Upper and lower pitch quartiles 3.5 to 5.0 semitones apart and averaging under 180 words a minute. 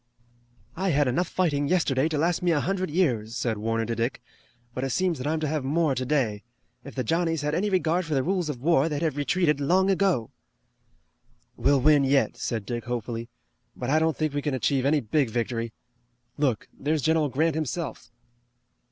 No: average, 4.3 semitones; average, 195 wpm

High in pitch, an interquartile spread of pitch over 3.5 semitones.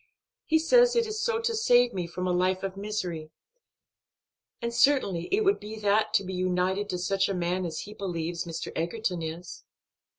Yes: high, 195 Hz; average, 5.2 semitones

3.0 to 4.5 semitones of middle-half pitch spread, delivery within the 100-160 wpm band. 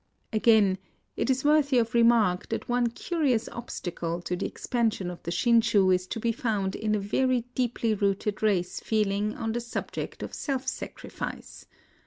No: average, 3.4 semitones; average, 170 wpm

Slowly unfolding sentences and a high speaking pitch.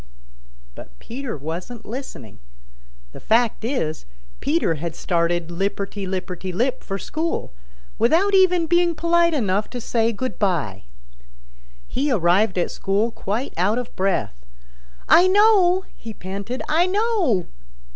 Yes: slow, 125 wpm; high, 225 Hz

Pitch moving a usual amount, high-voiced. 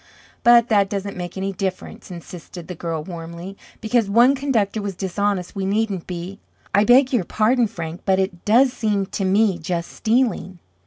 Yes: average, 3.5 semitones; high, 195 Hz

